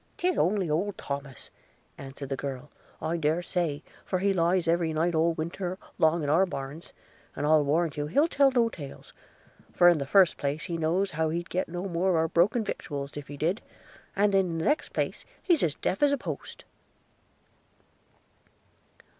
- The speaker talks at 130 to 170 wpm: No, average, 190 wpm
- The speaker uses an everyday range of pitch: Yes, average, 4.0 semitones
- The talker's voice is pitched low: No, medium, 170 Hz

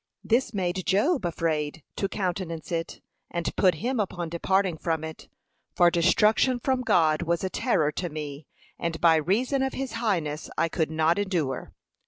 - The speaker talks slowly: No, average, 165 wpm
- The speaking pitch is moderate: Yes, medium, 175 Hz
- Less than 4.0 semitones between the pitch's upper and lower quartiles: No, average, 4.3 semitones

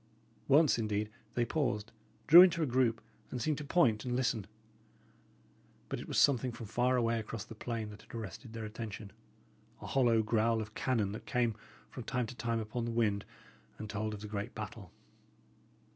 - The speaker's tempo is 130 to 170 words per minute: No, average, 185 wpm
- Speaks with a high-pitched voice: No, low, 115 Hz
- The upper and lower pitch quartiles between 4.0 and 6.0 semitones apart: No, narrow, 2.6 semitones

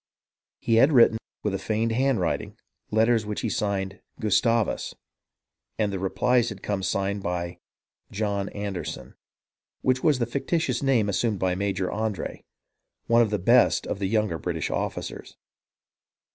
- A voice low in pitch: Yes, low, 105 Hz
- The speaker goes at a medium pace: Yes, average, 145 wpm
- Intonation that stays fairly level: No, average, 3.2 semitones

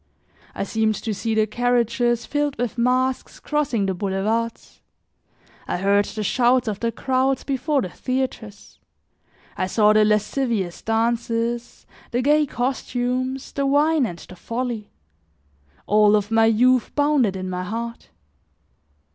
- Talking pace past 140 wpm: No, slow, 135 wpm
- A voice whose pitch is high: Yes, high, 235 Hz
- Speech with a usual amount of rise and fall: Yes, average, 3.3 semitones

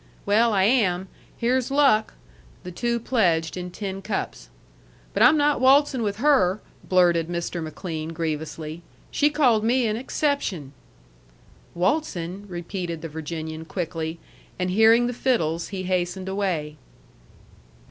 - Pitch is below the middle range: No, high, 190 Hz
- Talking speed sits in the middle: No, slow, 125 wpm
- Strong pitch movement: Yes, wide, 6.0 semitones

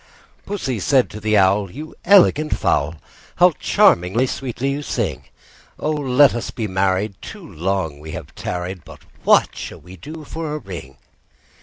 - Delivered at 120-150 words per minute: No, average, 165 wpm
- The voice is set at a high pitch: No, low, 110 Hz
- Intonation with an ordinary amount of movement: No, wide, 8.2 semitones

